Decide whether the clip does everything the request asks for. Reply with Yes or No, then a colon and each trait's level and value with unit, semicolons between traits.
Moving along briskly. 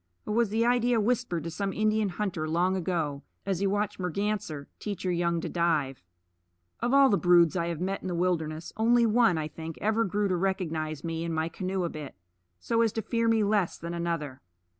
Yes: fast, 210 wpm